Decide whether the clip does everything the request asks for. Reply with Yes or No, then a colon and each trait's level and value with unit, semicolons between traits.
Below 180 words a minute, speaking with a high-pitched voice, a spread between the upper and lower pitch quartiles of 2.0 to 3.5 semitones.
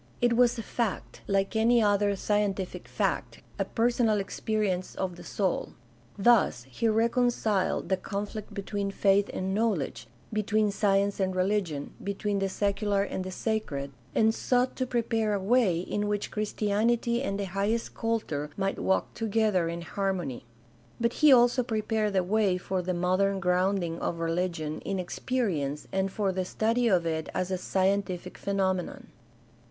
Yes: average, 155 wpm; high, 200 Hz; average, 3.0 semitones